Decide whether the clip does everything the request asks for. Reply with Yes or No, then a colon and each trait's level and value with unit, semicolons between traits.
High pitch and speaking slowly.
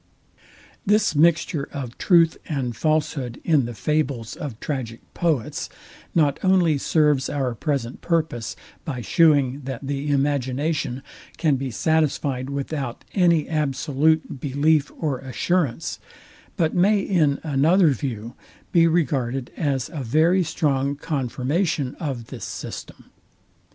No: medium, 145 Hz; slow, 120 wpm